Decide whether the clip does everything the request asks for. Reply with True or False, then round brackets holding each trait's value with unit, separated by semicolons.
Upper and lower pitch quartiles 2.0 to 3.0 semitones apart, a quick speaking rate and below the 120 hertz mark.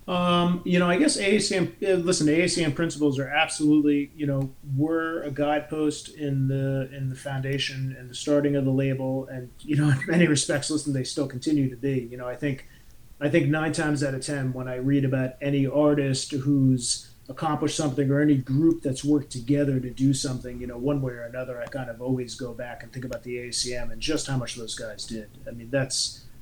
False (2.7 semitones; 220 wpm; 140 Hz)